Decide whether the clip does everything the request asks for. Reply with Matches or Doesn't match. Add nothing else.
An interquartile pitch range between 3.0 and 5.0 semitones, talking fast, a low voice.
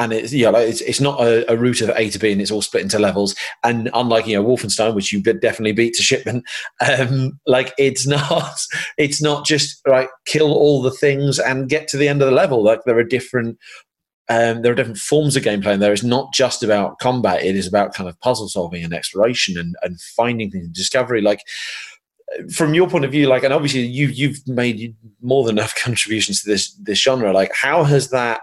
Matches